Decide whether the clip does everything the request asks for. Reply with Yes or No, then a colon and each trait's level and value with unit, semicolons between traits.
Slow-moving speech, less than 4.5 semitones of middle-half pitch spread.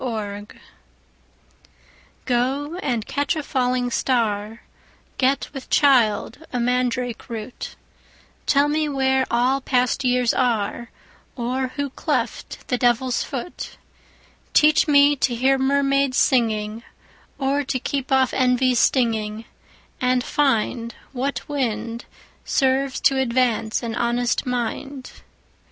Yes: slow, 115 wpm; narrow, 2.4 semitones